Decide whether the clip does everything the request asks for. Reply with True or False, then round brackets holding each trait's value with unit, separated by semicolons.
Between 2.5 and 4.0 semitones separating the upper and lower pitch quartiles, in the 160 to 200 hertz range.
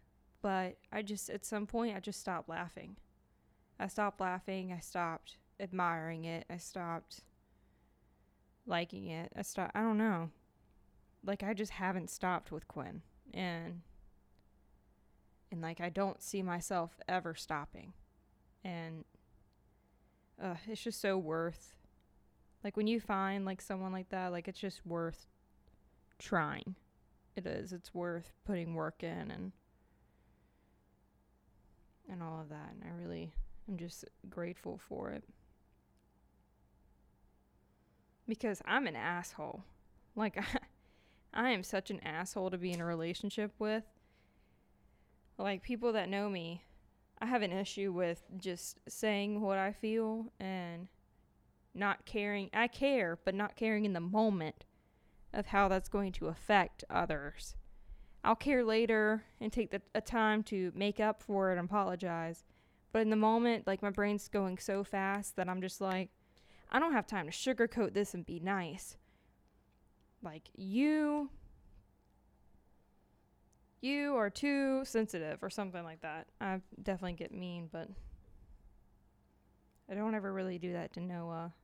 True (3.7 semitones; 190 Hz)